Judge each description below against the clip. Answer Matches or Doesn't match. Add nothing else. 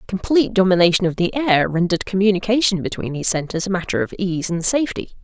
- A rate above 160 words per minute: Matches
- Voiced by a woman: Matches